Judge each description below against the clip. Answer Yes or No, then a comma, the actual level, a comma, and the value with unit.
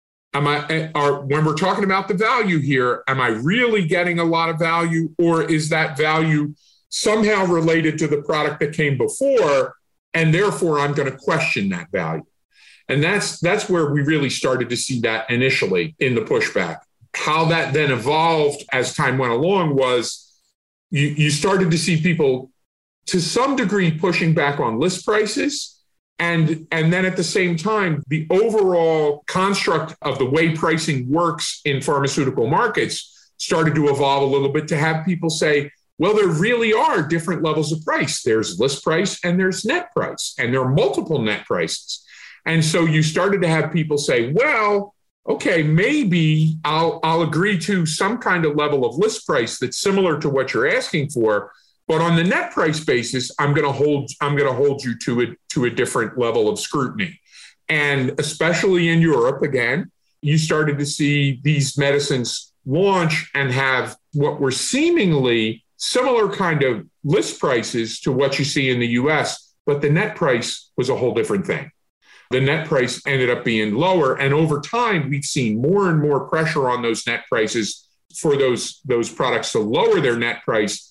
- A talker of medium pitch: Yes, medium, 155 Hz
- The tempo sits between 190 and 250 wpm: No, average, 180 wpm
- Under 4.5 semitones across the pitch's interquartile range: Yes, average, 4.1 semitones